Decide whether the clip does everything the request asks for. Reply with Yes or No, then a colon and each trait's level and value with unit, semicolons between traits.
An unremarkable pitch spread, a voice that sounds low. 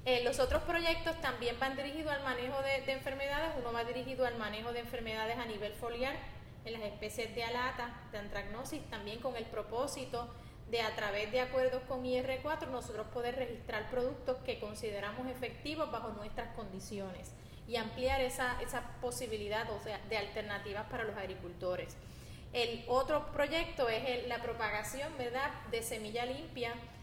No: average, 3.2 semitones; high, 245 Hz